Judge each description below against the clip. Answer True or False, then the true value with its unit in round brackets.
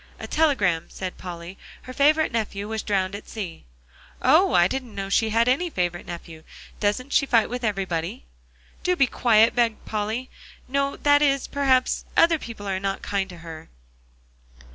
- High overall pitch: True (220 Hz)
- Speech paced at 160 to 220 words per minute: True (165 wpm)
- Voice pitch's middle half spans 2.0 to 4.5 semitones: False (5.5 semitones)